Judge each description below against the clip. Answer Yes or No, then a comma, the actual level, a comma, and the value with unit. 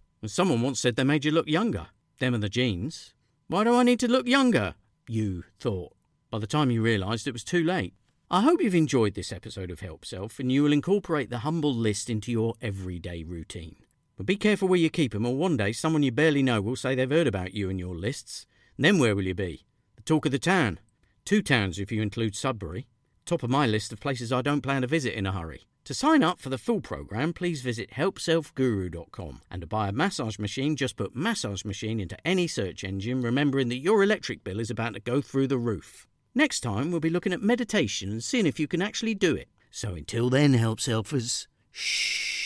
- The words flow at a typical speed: No, fast, 225 wpm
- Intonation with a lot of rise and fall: Yes, wide, 7.0 semitones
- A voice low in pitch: Yes, low, 125 Hz